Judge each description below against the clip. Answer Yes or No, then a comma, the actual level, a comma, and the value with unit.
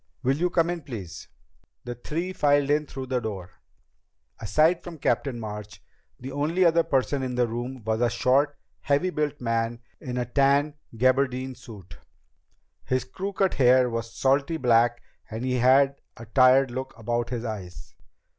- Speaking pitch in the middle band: No, low, 130 Hz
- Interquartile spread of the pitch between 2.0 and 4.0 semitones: Yes, average, 3.4 semitones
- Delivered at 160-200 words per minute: Yes, average, 165 wpm